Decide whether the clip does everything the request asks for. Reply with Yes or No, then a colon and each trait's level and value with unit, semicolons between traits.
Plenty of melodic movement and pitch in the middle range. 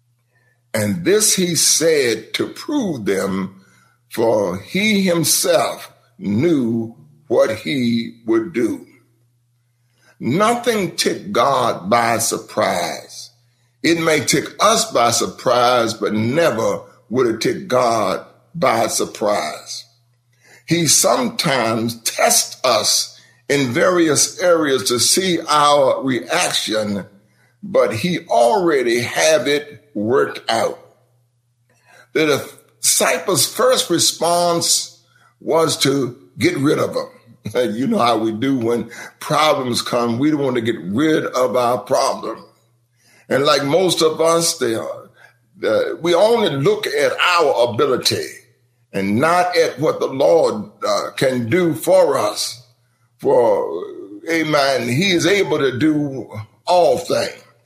Yes: wide, 6.8 semitones; medium, 145 Hz